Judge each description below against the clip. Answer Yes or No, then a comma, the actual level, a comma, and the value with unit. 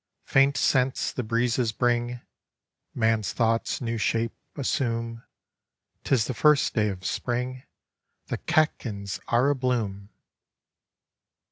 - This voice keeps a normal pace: No, slow, 110 wpm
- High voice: No, low, 120 Hz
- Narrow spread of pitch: Yes, narrow, 2.3 semitones